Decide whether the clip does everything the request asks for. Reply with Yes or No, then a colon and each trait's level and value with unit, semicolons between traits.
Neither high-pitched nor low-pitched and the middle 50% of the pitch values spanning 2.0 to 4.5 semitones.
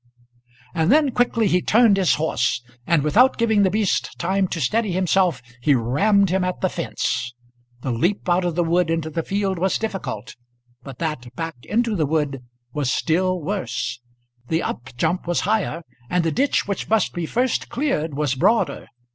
No: medium, 175 Hz; average, 4.9 semitones